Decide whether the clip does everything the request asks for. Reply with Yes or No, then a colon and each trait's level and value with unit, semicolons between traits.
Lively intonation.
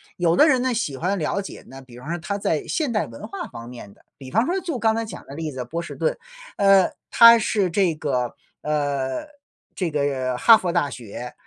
Yes: wide, 8.1 semitones